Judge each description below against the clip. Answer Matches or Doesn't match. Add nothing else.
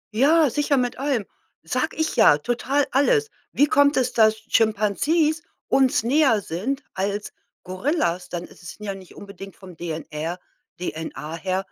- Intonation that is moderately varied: Doesn't match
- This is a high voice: Matches